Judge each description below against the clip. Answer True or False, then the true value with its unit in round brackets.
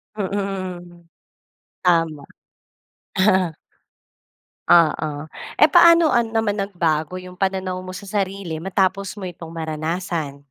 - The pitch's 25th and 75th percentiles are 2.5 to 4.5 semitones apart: True (3.1 semitones)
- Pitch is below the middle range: False (185 Hz)